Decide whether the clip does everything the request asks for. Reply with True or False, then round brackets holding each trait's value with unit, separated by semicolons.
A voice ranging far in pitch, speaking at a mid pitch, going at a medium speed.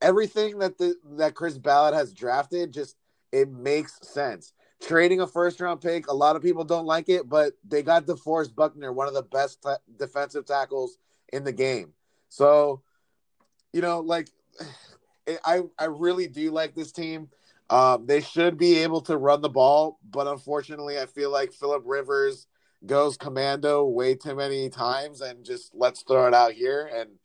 False (3.3 semitones; 150 Hz; 180 wpm)